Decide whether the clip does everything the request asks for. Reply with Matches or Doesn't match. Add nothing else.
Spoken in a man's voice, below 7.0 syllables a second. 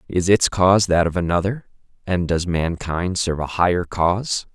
Matches